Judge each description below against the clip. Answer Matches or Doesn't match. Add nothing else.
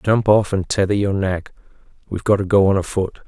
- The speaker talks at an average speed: Doesn't match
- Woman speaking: Doesn't match